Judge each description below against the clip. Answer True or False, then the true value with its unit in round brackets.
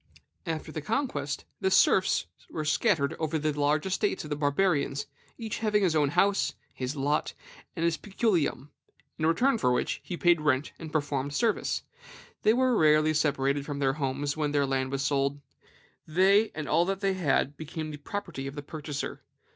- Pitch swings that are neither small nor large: True (4.6 semitones)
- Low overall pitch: False (155 Hz)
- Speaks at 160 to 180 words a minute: True (175 wpm)